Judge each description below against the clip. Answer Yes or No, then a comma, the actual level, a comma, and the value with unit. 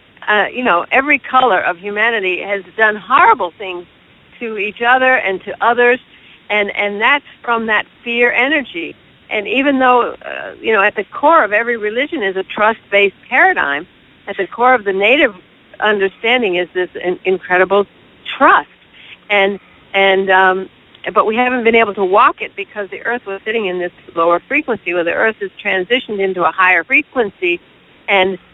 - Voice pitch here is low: No, high, 210 Hz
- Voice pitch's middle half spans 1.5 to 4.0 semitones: No, average, 4.5 semitones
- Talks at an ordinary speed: Yes, average, 175 wpm